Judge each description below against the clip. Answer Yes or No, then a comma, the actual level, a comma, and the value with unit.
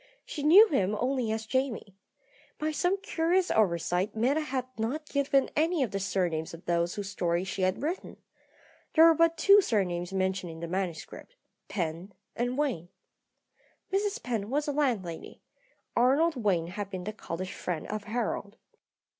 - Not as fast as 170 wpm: Yes, average, 160 wpm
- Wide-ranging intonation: Yes, wide, 7.9 semitones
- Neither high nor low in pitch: No, high, 220 Hz